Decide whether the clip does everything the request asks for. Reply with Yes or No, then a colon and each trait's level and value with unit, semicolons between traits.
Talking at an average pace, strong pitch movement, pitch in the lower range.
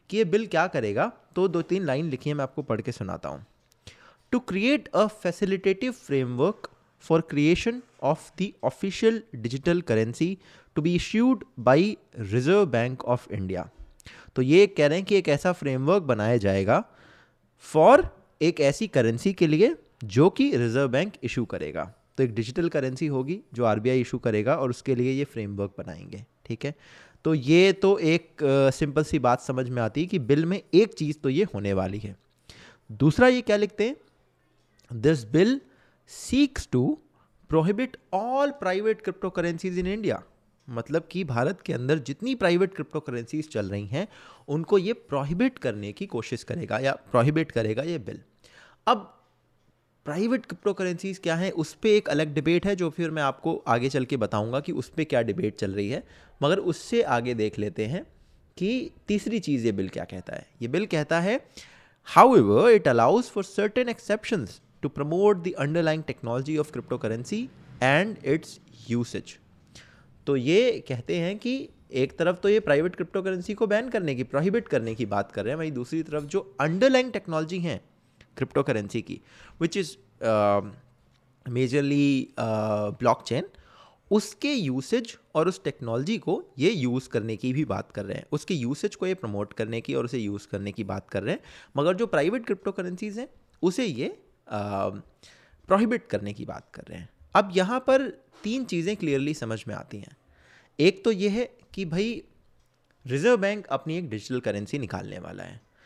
No: average, 175 wpm; wide, 8.0 semitones; medium, 155 Hz